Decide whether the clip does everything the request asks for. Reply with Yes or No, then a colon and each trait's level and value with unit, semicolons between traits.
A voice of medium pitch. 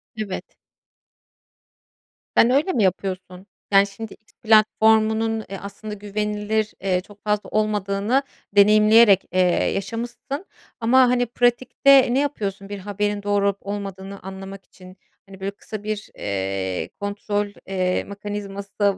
No: high, 205 Hz